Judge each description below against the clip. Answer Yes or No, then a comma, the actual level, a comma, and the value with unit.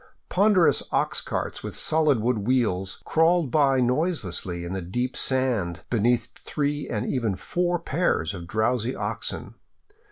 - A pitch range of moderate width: No, wide, 6.6 semitones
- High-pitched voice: No, low, 125 Hz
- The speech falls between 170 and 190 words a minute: No, slow, 135 wpm